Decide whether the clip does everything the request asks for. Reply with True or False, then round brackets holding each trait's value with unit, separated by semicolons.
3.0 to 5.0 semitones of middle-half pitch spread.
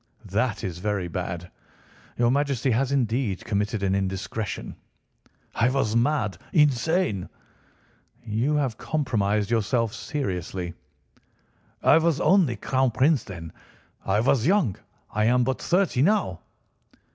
False (5.6 semitones)